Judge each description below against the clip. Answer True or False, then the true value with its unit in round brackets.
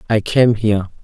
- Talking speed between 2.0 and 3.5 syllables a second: False (5.3 syllables/s)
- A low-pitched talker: True (110 Hz)